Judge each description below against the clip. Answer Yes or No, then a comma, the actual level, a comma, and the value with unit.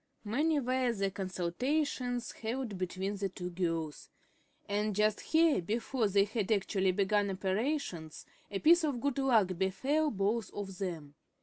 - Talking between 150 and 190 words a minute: No, average, 140 wpm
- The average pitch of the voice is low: No, high, 205 Hz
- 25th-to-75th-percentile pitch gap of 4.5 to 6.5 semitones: Yes, average, 5.1 semitones